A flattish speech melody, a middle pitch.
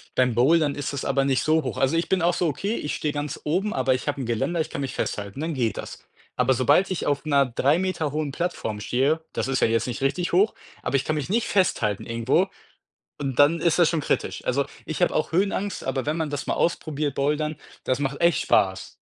No: average, 3.9 semitones; medium, 145 Hz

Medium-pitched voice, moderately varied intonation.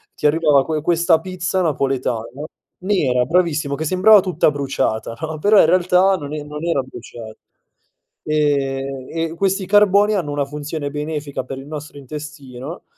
Yes: medium, 150 Hz; average, 4.2 semitones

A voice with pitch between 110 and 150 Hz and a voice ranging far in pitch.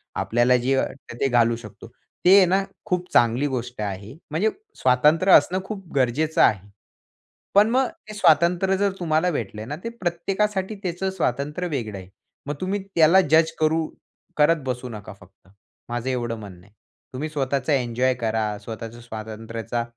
Yes: medium, 140 Hz; wide, 7.2 semitones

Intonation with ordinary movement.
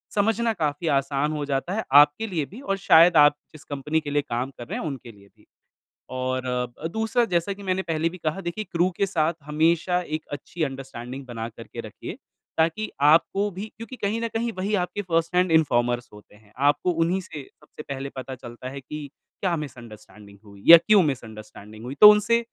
No: wide, 6.3 semitones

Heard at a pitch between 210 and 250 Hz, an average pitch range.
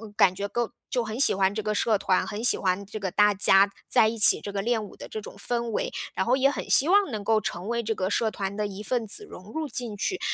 Yes: high, 215 Hz; average, 3.0 semitones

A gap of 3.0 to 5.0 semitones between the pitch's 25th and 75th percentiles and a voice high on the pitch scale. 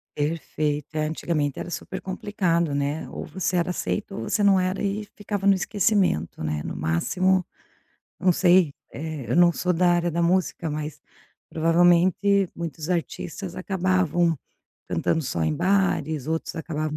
No: average, 3.4 semitones; medium, 170 Hz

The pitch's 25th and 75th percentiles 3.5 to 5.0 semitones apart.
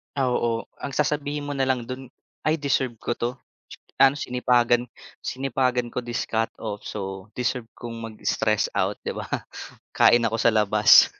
No: average, 2.8 semitones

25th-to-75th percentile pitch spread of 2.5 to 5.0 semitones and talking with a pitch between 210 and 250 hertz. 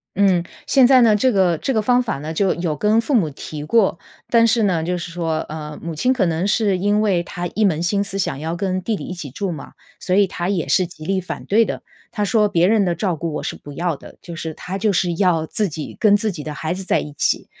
No: average, 4.0 semitones; medium, 185 Hz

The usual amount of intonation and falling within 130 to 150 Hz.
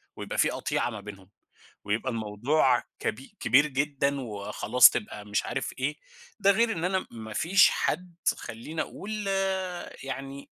No: wide, 6.6 semitones; low, 135 Hz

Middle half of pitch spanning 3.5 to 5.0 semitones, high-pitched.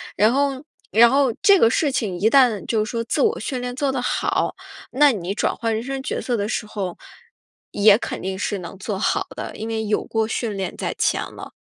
Yes: average, 4.1 semitones; high, 225 Hz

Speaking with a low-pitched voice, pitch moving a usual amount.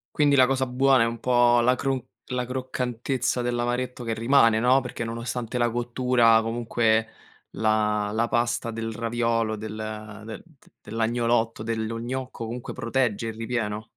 No: low, 115 Hz; narrow, 1.8 semitones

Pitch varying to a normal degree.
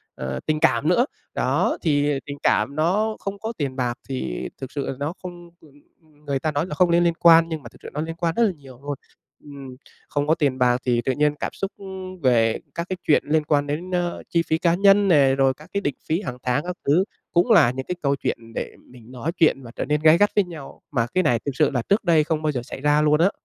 Yes: average, 4.3 semitones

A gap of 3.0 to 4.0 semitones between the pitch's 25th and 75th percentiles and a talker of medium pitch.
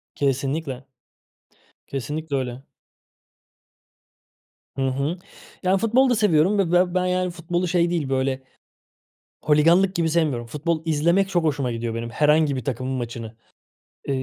No: average, 4.8 semitones; medium, 155 Hz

